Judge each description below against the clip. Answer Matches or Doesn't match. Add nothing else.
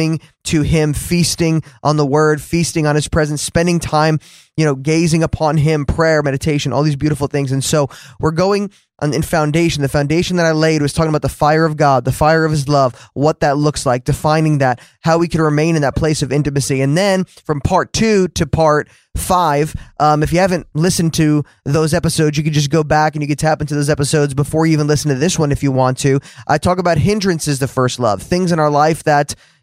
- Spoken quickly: Matches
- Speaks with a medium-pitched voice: Matches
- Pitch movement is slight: Matches